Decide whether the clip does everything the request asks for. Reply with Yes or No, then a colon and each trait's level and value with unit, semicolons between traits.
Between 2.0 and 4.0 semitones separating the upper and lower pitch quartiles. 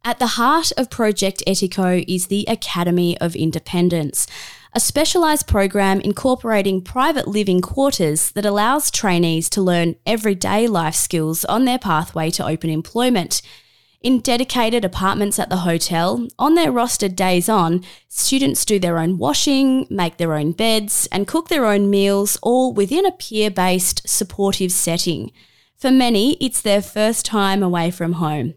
No: wide, 5.5 semitones